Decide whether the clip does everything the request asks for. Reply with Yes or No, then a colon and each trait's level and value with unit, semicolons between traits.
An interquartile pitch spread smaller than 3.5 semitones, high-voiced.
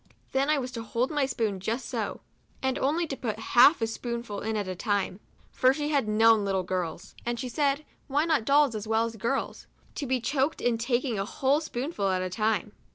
No: average, 4.2 semitones; high, 240 Hz